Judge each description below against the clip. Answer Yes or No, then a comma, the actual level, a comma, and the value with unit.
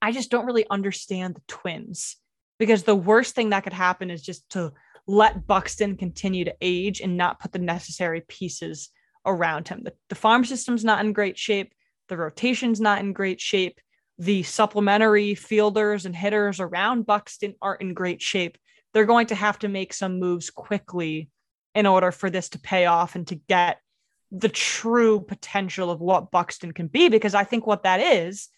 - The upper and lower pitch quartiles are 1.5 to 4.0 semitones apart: Yes, average, 2.8 semitones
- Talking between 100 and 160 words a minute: No, average, 185 wpm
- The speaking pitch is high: Yes, high, 195 Hz